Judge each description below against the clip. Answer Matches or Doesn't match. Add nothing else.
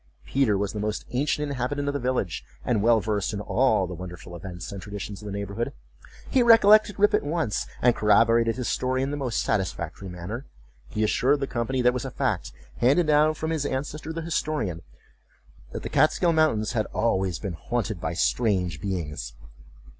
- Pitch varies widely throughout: Matches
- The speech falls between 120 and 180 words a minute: Doesn't match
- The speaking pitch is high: Doesn't match